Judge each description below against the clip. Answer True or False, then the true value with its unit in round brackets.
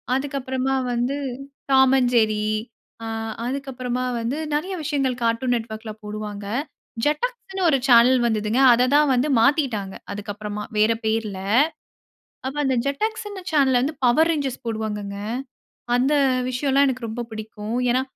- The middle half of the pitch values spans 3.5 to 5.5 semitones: True (4.1 semitones)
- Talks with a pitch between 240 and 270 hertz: True (250 Hz)